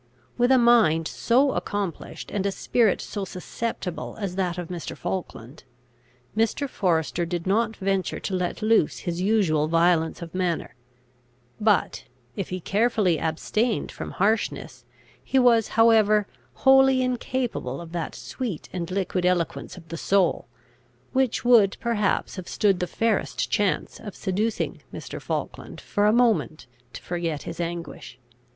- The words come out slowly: No, average, 145 wpm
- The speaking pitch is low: No, high, 195 Hz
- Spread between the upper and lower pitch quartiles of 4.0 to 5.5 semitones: Yes, average, 4.7 semitones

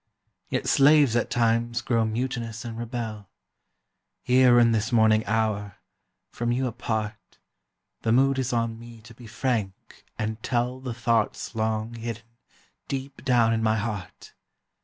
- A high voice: No, low, 115 Hz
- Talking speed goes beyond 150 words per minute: No, average, 140 wpm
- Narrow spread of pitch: Yes, narrow, 1.7 semitones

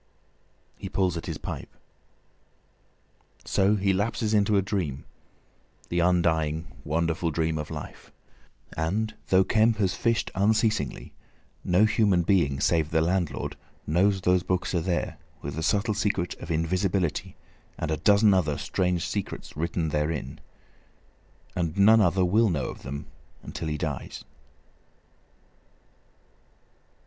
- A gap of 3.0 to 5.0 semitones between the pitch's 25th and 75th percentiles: Yes, average, 3.9 semitones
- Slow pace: Yes, slow, 130 wpm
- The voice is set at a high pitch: No, very low, 90 Hz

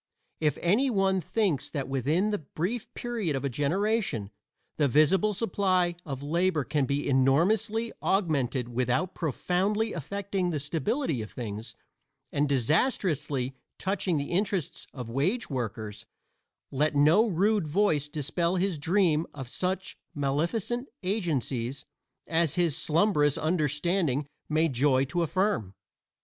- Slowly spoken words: Yes, slow, 125 wpm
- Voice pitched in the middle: Yes, medium, 160 Hz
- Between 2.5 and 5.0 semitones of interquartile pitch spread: No, wide, 5.6 semitones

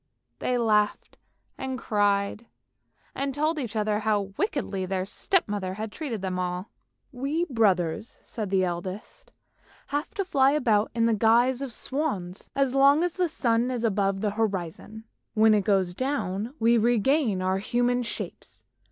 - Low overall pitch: No, high, 220 Hz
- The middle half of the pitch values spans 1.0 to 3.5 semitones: No, average, 4.9 semitones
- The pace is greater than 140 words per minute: Yes, average, 160 wpm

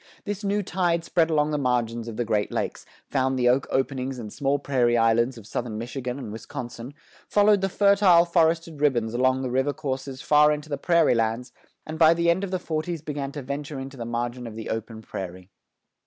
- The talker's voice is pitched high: No, low, 135 Hz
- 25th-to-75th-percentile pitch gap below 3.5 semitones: No, average, 5.1 semitones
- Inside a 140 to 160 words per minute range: No, fast, 205 wpm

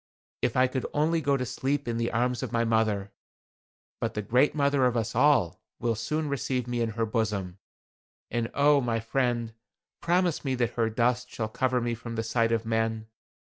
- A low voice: Yes, low, 120 Hz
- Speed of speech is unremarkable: Yes, average, 195 wpm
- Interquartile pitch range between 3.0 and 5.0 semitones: No, narrow, 2.6 semitones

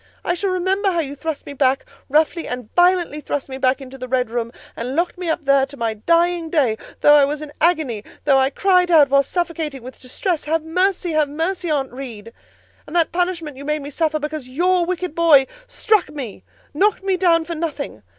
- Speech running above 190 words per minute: Yes, average, 200 wpm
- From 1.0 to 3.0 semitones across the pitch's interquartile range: No, average, 4.4 semitones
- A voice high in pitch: Yes, very high, 305 Hz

